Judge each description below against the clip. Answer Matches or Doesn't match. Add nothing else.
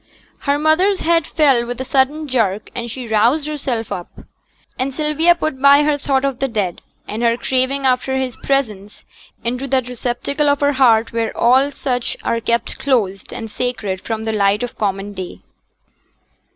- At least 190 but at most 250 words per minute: Doesn't match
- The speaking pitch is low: Doesn't match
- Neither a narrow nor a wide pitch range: Matches